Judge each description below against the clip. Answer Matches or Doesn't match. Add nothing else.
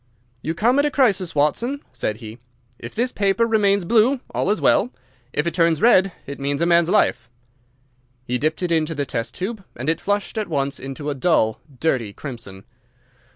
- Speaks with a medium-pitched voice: Matches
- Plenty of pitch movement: Matches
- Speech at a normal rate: Matches